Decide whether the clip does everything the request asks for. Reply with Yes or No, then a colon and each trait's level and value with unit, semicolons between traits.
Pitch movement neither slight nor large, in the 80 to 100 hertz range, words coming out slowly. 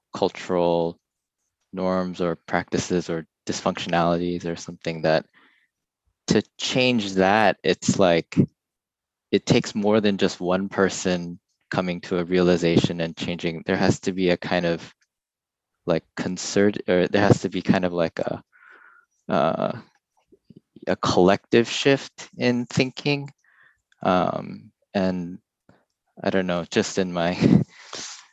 Yes: average, 3.0 semitones; very low, 90 Hz; slow, 125 wpm